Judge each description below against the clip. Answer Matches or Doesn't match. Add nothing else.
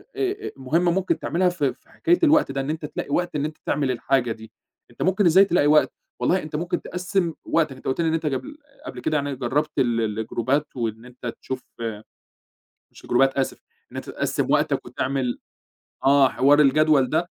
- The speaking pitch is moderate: Matches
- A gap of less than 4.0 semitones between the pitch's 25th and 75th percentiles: Doesn't match